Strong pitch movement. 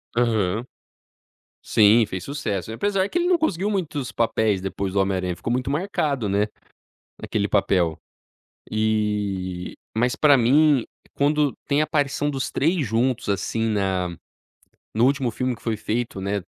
Yes: wide, 6.0 semitones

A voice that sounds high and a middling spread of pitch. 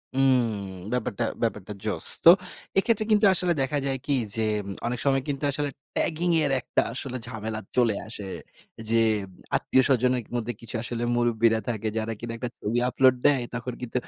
No: low, 125 Hz; average, 3.0 semitones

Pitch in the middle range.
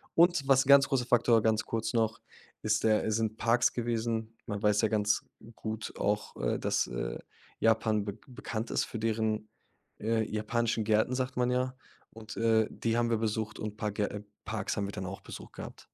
No: low, 110 Hz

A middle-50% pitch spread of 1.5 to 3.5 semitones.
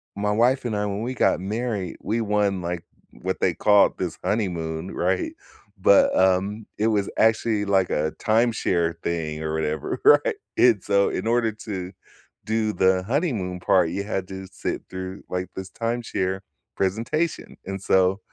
Yes: average, 3.2 semitones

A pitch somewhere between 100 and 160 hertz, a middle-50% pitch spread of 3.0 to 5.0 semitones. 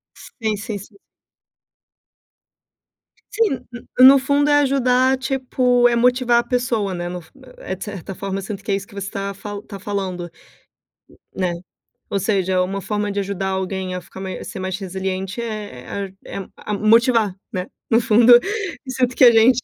No: high, 205 Hz; average, 4.4 semitones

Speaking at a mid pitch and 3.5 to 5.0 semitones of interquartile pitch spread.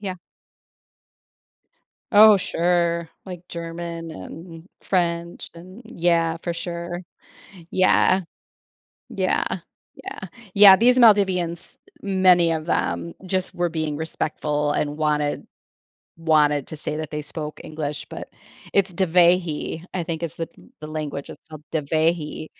No: medium, 170 Hz; narrow, 2.5 semitones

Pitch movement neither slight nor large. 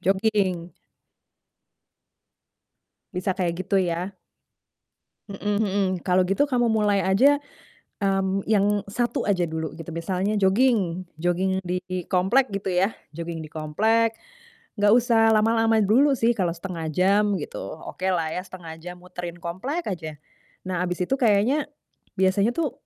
Yes: average, 3.4 semitones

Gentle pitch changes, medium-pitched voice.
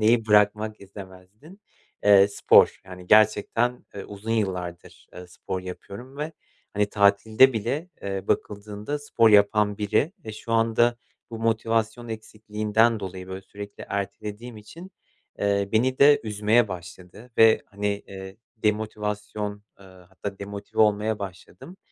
No: narrow, 2.1 semitones; low, 105 Hz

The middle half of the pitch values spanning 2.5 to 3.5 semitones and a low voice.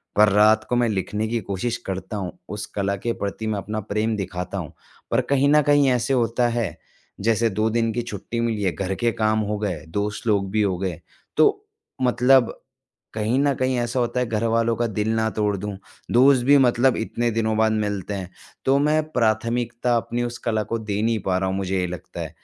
Yes: average, 2.8 semitones; low, 110 Hz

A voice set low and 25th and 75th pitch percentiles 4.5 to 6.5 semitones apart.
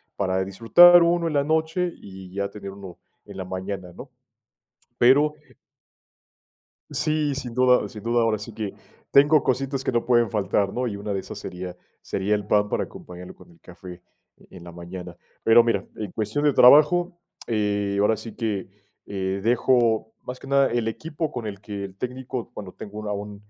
Yes: low, 110 Hz; average, 4.9 semitones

